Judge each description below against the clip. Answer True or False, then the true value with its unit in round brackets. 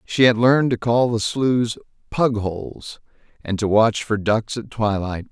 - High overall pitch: False (115 Hz)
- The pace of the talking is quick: False (170 wpm)